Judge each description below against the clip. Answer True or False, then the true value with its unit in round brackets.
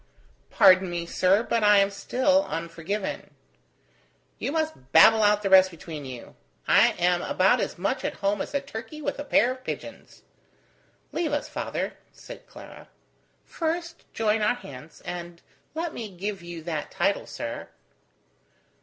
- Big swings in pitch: True (7.0 semitones)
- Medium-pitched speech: False (200 Hz)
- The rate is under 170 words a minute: True (155 wpm)